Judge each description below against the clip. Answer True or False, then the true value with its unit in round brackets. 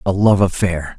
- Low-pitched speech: True (95 Hz)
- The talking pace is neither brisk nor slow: True (180 wpm)